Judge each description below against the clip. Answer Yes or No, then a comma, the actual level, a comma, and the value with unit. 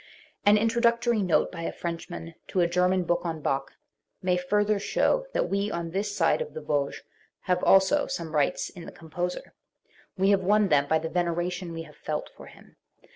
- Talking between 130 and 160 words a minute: No, average, 190 wpm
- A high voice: No, medium, 180 Hz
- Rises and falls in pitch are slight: No, average, 3.4 semitones